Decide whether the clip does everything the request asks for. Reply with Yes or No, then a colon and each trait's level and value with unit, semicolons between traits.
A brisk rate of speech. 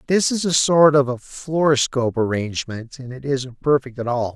No: average, 195 wpm